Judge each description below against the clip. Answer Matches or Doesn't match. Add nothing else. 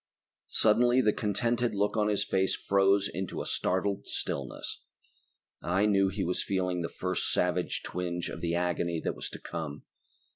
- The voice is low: Matches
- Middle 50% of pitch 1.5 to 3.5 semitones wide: Matches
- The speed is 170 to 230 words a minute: Doesn't match